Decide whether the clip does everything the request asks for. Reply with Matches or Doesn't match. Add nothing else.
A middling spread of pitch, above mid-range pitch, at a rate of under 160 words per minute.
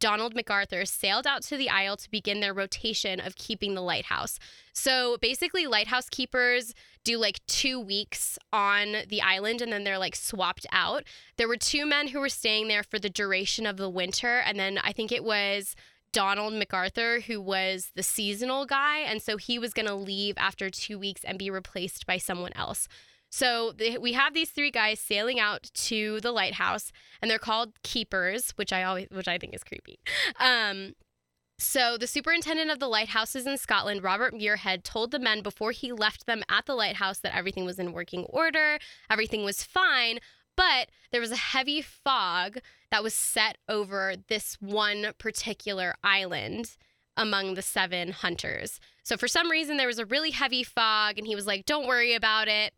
Doesn't match